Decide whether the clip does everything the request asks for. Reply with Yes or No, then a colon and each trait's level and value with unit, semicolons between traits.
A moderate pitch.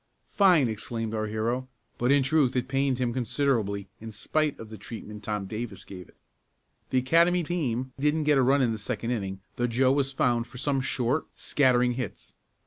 No: low, 125 Hz